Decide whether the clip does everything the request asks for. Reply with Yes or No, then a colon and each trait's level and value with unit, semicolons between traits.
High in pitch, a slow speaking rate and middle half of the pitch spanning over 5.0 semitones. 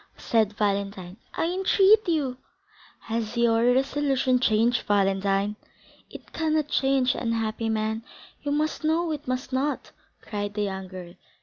Yes: high, 235 Hz; slow, 125 wpm; wide, 5.6 semitones